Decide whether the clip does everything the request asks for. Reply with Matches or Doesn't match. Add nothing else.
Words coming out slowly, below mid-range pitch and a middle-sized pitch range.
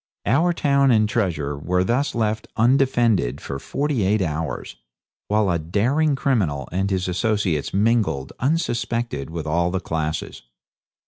Doesn't match